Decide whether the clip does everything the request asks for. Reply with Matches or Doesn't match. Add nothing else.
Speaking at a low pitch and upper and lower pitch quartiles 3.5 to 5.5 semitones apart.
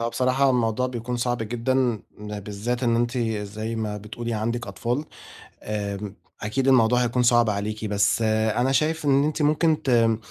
Doesn't match